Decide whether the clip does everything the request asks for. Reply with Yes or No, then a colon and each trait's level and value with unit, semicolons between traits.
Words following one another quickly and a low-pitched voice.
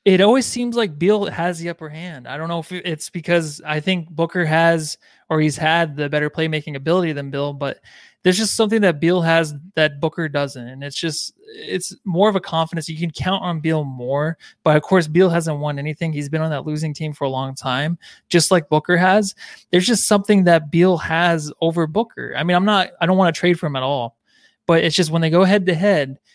No: fast, 235 wpm; medium, 165 Hz